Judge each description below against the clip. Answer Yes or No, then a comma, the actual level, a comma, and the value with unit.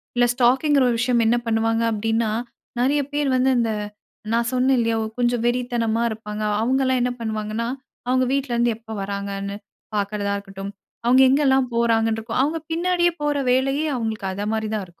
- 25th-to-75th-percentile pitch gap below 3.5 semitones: Yes, average, 2.8 semitones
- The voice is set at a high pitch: Yes, high, 235 Hz